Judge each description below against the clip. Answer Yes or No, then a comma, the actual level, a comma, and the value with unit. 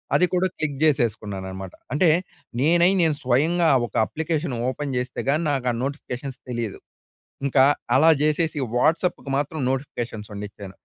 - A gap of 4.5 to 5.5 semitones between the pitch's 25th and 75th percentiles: Yes, average, 4.8 semitones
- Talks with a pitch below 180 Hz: Yes, medium, 140 Hz